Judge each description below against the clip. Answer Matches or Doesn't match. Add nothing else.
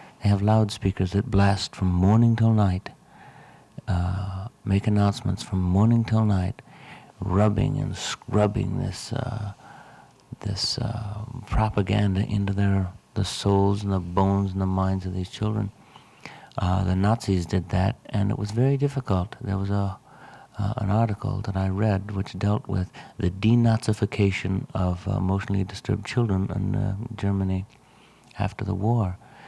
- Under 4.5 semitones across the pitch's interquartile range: Matches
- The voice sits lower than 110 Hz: Matches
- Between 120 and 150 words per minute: Matches